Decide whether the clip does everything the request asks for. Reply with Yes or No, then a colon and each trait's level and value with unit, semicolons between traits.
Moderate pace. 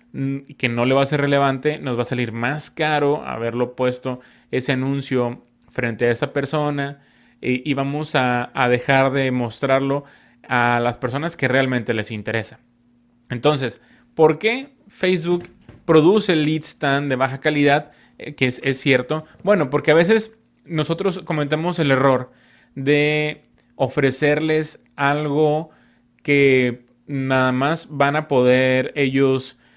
Yes: average, 135 wpm